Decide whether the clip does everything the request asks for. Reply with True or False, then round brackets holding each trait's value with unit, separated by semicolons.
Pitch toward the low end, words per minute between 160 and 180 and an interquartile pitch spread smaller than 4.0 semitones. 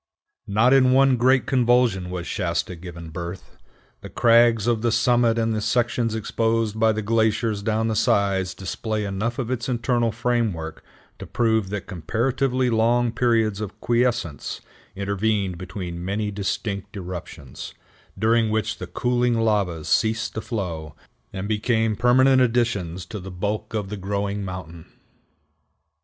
False (110 Hz; 145 wpm; 3.6 semitones)